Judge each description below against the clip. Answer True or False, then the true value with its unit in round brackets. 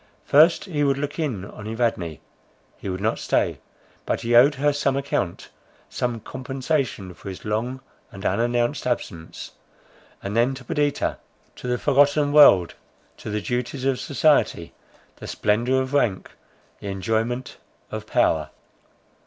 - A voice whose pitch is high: False (125 Hz)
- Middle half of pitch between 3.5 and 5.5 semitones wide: True (4.9 semitones)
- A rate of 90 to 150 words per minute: True (145 wpm)